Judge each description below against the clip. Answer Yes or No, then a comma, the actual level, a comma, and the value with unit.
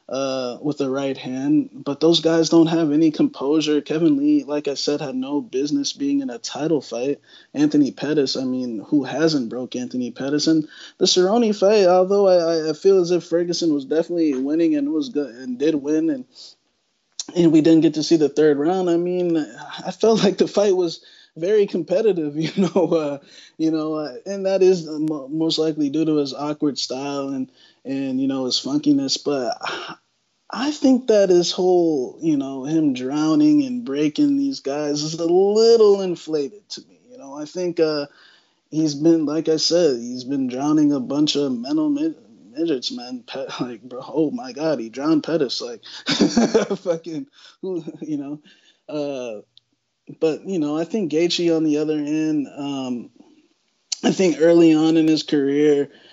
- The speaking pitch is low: No, medium, 165 Hz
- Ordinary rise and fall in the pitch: No, wide, 8.1 semitones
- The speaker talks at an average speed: Yes, average, 180 wpm